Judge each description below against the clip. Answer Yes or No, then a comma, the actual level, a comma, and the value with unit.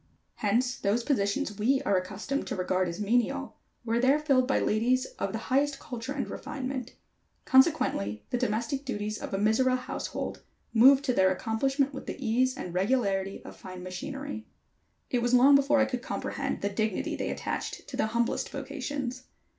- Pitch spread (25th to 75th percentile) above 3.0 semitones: Yes, average, 4.5 semitones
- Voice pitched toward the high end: Yes, high, 245 Hz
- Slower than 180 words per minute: Yes, average, 170 wpm